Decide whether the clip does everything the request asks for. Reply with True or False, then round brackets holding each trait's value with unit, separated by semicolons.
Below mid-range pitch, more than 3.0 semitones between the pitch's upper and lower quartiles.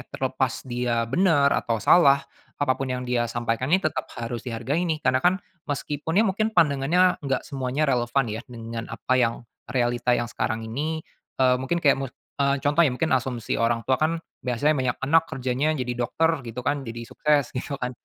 True (130 Hz; 3.7 semitones)